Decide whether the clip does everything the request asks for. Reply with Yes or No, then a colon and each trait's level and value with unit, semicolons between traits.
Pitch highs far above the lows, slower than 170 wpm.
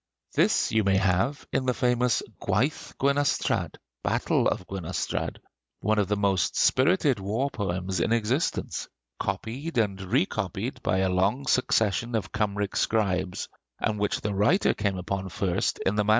No: average, 4.3 semitones; average, 150 wpm